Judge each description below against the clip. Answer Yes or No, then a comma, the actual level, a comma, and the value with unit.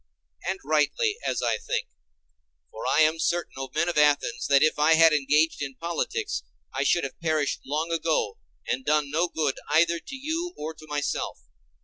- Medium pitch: Yes, medium, 155 Hz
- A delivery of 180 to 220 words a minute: Yes, average, 185 wpm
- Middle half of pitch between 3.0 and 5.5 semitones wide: No, narrow, 2.6 semitones